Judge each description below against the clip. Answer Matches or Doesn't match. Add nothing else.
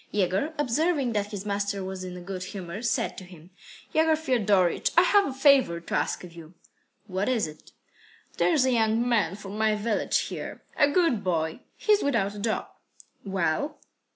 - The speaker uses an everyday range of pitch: Doesn't match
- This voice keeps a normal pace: Matches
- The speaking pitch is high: Matches